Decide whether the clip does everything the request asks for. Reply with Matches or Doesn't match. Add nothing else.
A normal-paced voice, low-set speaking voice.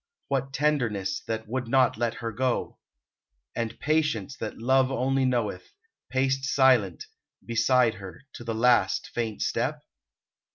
Doesn't match